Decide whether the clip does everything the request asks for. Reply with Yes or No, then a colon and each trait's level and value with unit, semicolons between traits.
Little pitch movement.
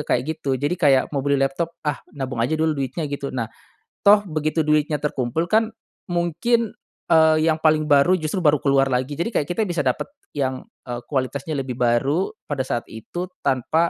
No: average, 3.3 semitones